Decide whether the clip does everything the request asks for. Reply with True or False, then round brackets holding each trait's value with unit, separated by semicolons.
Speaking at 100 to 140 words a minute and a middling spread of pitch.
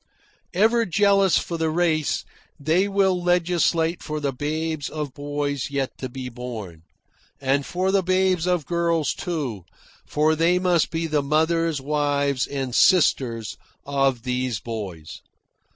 True (135 wpm; 4.4 semitones)